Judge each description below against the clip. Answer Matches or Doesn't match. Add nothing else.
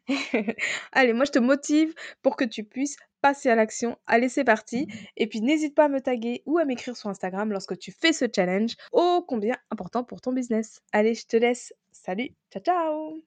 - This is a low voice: Doesn't match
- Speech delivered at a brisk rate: Doesn't match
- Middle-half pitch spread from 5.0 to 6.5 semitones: Doesn't match